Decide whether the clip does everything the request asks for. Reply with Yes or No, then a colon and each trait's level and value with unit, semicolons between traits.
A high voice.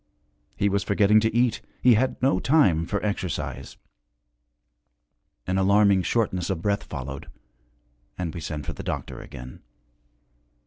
No: very low, 95 Hz